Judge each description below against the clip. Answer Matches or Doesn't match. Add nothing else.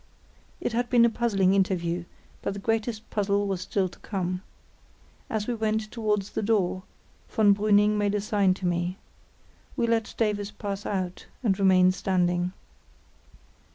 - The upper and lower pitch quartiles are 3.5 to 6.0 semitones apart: Doesn't match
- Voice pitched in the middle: Doesn't match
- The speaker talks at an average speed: Matches